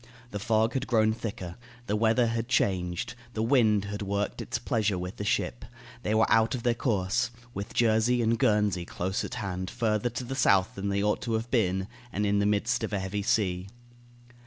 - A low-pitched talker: Yes, low, 105 Hz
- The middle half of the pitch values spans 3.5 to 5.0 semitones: No, average, 2.7 semitones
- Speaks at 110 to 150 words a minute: No, fast, 205 wpm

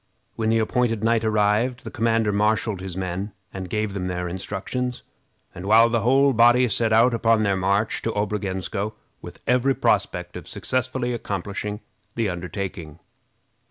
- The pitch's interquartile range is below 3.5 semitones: Yes, average, 3.1 semitones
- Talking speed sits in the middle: Yes, average, 150 wpm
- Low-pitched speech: Yes, low, 110 Hz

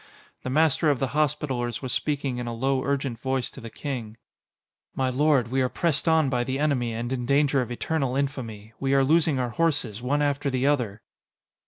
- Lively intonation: No, average, 3.0 semitones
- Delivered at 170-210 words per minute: Yes, average, 200 wpm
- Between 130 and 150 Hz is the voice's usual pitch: Yes, low, 135 Hz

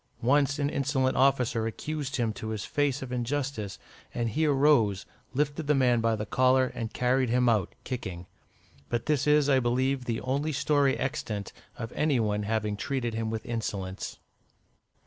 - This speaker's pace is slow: No, average, 165 wpm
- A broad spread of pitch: No, average, 3.8 semitones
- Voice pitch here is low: Yes, low, 125 Hz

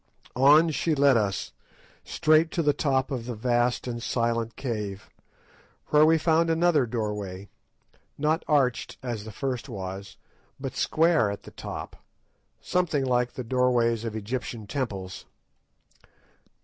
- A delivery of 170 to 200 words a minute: No, slow, 135 wpm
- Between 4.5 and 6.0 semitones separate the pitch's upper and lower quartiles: Yes, average, 5.1 semitones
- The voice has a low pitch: Yes, low, 125 Hz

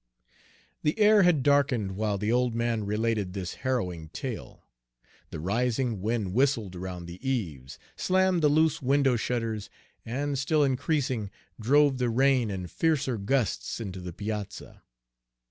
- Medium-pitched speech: No, low, 120 Hz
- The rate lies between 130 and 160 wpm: Yes, average, 140 wpm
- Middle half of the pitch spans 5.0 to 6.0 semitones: Yes, wide, 5.5 semitones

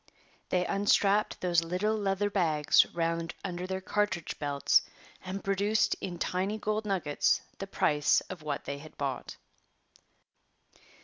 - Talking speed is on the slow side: Yes, slow, 130 wpm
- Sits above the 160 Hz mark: Yes, medium, 185 Hz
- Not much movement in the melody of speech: No, average, 3.3 semitones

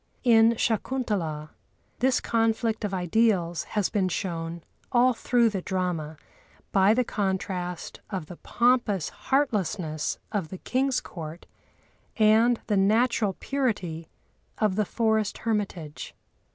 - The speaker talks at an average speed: No, slow, 115 wpm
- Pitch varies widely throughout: No, average, 4.5 semitones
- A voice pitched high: Yes, high, 205 Hz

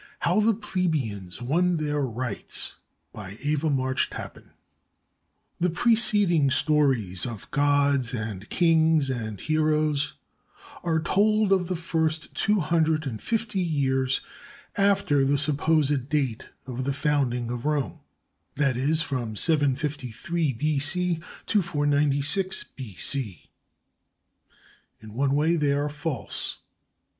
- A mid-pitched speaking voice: Yes, medium, 145 Hz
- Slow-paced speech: Yes, slow, 115 wpm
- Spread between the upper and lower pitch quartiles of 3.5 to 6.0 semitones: Yes, average, 3.9 semitones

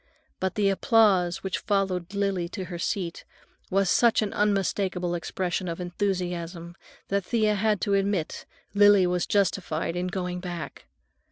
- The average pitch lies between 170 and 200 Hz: Yes, high, 190 Hz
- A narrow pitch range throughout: Yes, narrow, 2.2 semitones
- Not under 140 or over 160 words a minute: Yes, average, 145 wpm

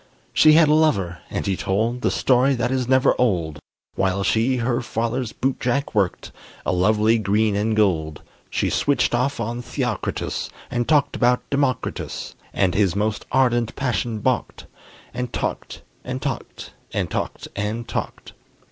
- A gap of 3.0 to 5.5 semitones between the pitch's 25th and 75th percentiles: Yes, average, 3.8 semitones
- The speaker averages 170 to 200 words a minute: No, average, 150 wpm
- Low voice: Yes, low, 115 Hz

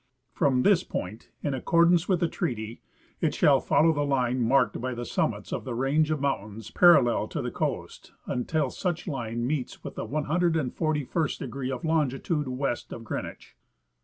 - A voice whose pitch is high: No, medium, 140 Hz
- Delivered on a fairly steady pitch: No, average, 4.4 semitones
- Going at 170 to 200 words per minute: Yes, average, 175 wpm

